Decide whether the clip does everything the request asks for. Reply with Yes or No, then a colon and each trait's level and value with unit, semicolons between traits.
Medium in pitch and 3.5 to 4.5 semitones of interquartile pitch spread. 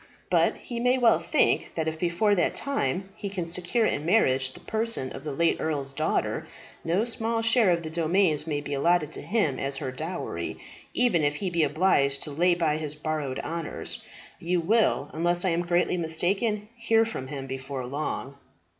No: medium, 170 Hz; average, 5.3 semitones